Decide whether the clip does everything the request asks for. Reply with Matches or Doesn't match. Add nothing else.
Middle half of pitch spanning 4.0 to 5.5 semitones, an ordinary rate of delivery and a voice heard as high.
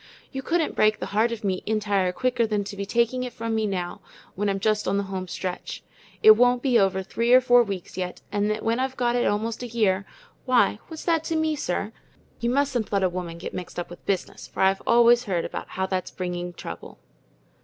Doesn't match